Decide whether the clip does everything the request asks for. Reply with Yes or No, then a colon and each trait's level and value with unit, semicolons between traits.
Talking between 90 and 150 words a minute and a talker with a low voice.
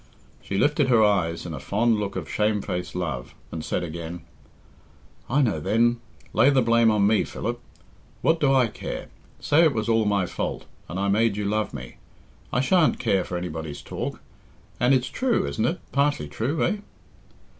No: average, 185 wpm; low, 105 Hz